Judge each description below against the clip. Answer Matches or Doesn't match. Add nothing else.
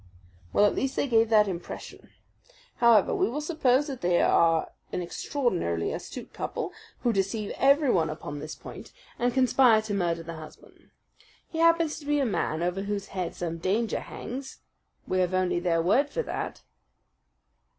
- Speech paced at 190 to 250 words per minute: Doesn't match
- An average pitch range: Doesn't match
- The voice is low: Doesn't match